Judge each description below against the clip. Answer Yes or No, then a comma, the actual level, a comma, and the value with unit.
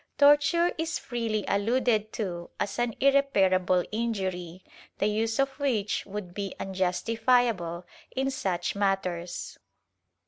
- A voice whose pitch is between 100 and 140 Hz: No, high, 210 Hz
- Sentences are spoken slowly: Yes, slow, 110 wpm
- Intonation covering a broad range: No, average, 4.8 semitones